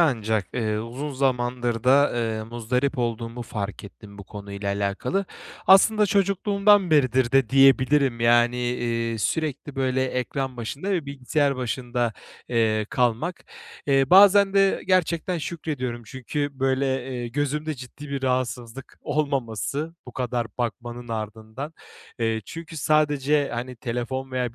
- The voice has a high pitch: No, low, 130 Hz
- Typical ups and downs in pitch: Yes, average, 3.8 semitones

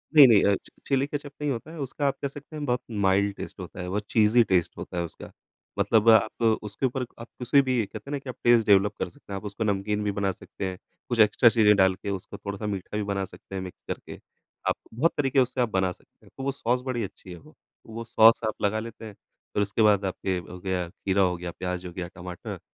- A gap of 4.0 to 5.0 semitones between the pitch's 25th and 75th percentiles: Yes, average, 4.4 semitones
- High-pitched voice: No, low, 105 Hz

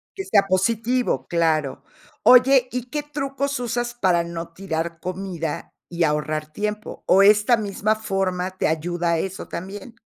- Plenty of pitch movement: Yes, wide, 6.0 semitones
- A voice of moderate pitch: No, high, 195 Hz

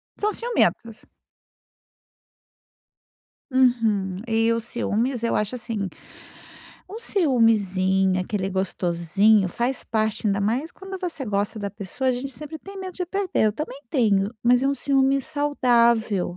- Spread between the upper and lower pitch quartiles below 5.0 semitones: No, wide, 5.4 semitones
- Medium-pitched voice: No, high, 230 Hz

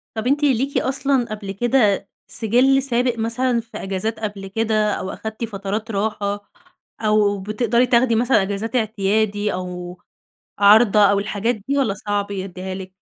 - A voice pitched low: No, high, 215 Hz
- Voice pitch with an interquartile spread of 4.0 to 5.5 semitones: No, average, 2.9 semitones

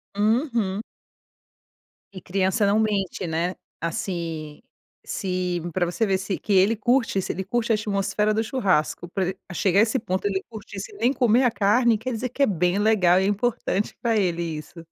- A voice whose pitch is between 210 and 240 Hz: No, high, 200 Hz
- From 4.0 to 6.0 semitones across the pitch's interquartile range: No, average, 3.5 semitones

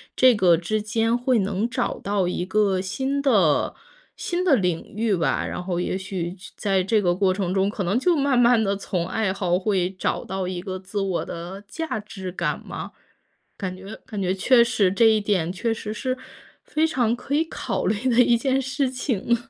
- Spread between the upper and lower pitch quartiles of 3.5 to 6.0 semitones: Yes, average, 4.3 semitones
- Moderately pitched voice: No, high, 205 Hz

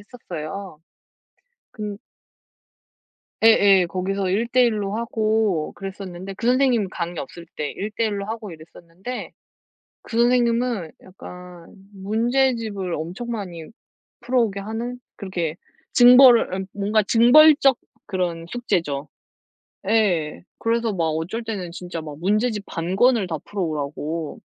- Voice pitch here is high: Yes, high, 200 Hz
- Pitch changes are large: No, average, 4.9 semitones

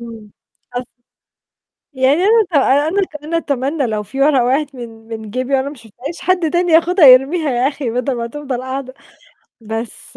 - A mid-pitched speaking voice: No, very high, 265 Hz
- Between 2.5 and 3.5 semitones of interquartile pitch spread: No, average, 4.0 semitones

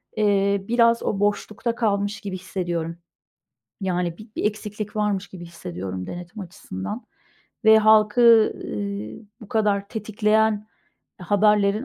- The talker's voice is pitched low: No, high, 205 Hz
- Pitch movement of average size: Yes, average, 3.2 semitones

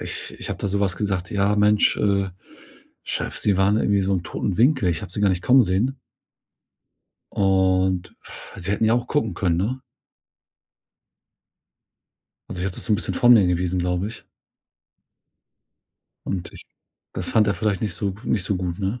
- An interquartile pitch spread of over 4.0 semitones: No, narrow, 2.5 semitones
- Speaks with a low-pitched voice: Yes, low, 100 Hz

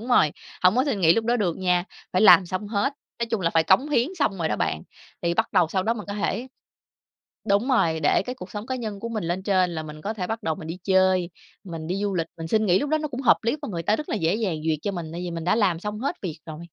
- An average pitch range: Yes, average, 4.7 semitones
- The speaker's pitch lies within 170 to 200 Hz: Yes, high, 190 Hz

